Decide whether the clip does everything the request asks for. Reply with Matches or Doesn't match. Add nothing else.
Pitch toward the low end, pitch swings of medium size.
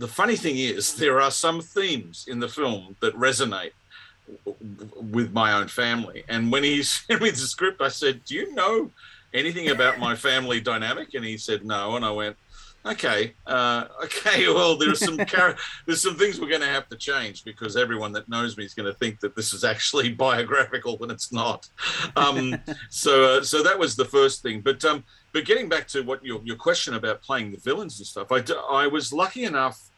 Doesn't match